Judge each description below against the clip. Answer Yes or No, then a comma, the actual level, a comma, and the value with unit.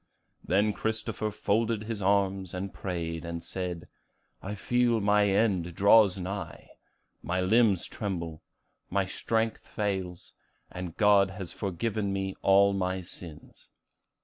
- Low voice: Yes, very low, 95 Hz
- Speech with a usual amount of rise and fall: No, narrow, 2.3 semitones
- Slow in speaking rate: Yes, slow, 120 wpm